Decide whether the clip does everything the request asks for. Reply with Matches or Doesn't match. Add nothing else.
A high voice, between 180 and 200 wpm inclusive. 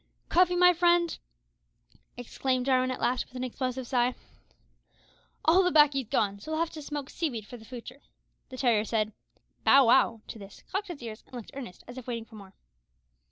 Matches